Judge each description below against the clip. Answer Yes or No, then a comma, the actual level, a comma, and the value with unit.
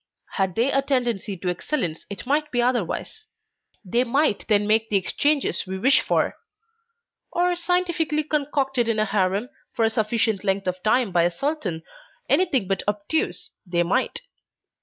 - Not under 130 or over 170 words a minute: Yes, average, 160 wpm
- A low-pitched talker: No, high, 230 Hz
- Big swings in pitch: Yes, wide, 6.5 semitones